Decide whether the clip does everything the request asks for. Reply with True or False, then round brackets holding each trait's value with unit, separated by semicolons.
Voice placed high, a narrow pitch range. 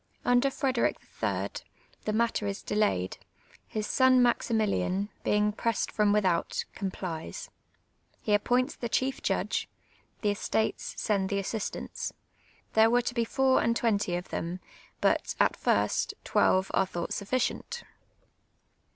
False (215 Hz; 3.5 semitones)